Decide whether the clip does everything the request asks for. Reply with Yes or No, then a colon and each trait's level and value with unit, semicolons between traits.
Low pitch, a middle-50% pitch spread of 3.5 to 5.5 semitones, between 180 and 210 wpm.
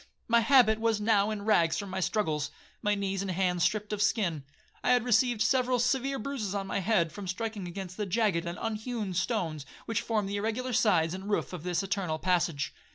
No: high, 205 Hz; average, 3.8 semitones; fast, 205 wpm